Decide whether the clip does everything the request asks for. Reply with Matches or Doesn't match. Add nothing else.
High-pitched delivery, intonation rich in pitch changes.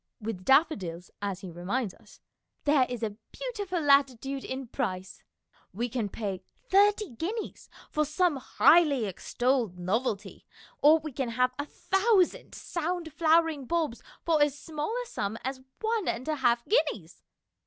Matches